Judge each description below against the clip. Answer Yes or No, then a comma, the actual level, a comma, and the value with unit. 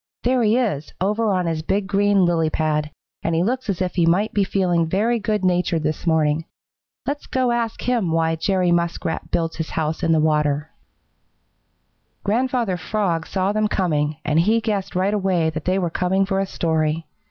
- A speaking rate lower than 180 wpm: No, average, 185 wpm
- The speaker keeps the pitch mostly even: No, average, 4.2 semitones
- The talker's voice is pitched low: No, medium, 180 Hz